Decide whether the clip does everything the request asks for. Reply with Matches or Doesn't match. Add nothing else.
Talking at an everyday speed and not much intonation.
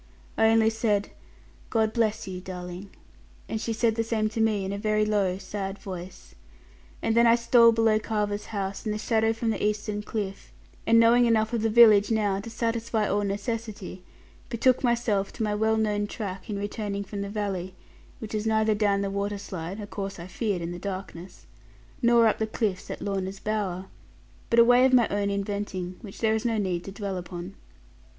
Matches